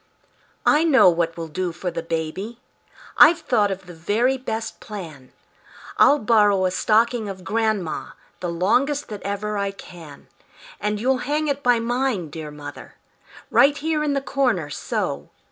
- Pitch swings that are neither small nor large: No, wide, 6.8 semitones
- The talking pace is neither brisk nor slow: Yes, average, 160 wpm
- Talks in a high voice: Yes, high, 210 Hz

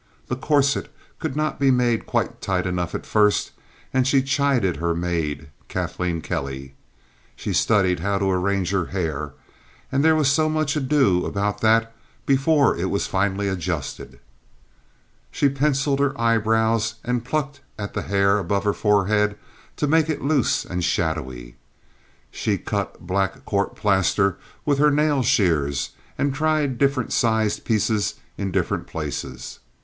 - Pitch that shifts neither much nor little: No, wide, 7.0 semitones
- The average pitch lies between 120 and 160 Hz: No, low, 105 Hz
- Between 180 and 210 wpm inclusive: No, average, 145 wpm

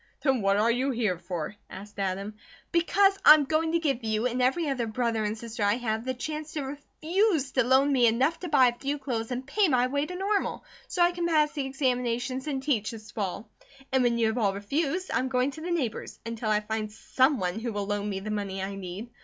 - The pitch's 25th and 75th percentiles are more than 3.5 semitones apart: Yes, average, 5.1 semitones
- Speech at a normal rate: No, fast, 235 wpm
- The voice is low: No, very high, 250 Hz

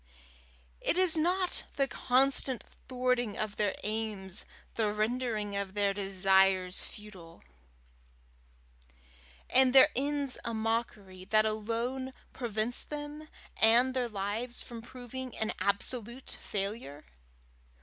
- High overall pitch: Yes, high, 225 Hz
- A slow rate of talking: Yes, slow, 110 wpm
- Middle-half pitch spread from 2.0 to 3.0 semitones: No, average, 4.1 semitones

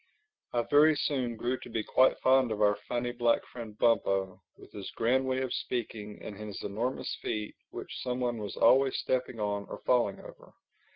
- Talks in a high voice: No, low, 120 Hz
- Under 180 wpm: No, average, 185 wpm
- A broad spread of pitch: No, average, 3.4 semitones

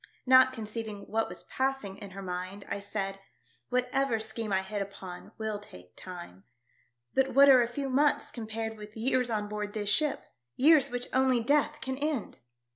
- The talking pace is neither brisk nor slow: Yes, average, 180 wpm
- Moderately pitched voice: No, high, 225 Hz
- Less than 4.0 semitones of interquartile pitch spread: No, average, 4.5 semitones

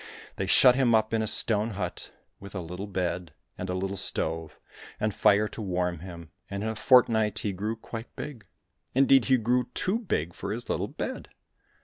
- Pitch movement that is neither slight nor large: Yes, average, 3.8 semitones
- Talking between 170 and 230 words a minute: Yes, average, 200 wpm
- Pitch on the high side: No, low, 105 Hz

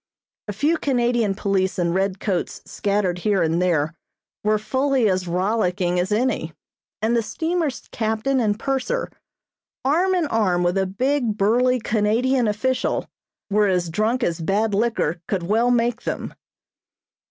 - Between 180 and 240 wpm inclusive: No, average, 145 wpm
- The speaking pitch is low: No, high, 215 Hz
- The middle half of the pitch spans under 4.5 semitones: No, average, 4.9 semitones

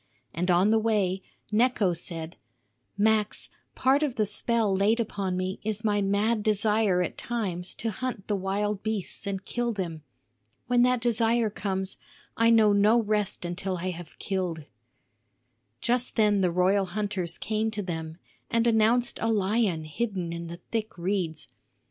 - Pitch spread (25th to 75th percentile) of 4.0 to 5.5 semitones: No, average, 3.3 semitones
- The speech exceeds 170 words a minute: No, average, 155 wpm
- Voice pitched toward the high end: Yes, high, 205 Hz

